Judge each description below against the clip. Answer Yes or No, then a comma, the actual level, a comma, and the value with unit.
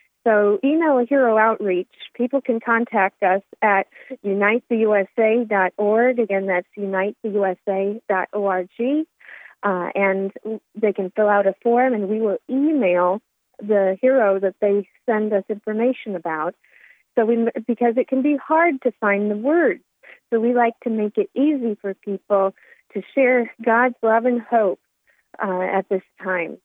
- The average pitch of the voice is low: No, high, 215 Hz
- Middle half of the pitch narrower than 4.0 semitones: Yes, average, 3.6 semitones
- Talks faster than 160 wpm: No, average, 140 wpm